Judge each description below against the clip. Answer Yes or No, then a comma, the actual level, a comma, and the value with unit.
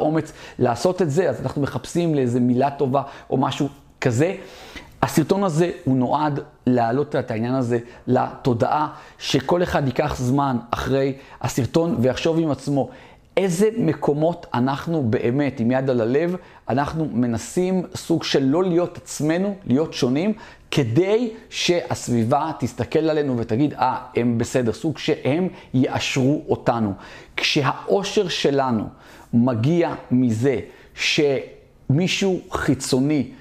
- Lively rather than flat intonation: No, average, 4.9 semitones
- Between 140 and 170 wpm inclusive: No, average, 120 wpm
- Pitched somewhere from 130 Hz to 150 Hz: Yes, medium, 140 Hz